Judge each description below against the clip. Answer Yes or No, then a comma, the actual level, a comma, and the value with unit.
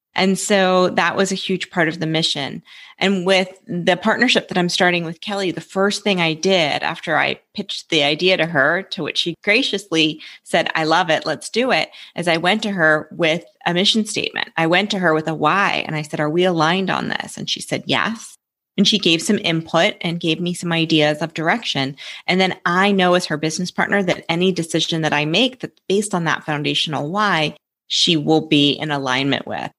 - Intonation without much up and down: No, average, 3.3 semitones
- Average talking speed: No, fast, 220 wpm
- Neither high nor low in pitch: Yes, medium, 175 Hz